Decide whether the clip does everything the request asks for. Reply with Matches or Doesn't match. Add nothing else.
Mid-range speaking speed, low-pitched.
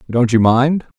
Matches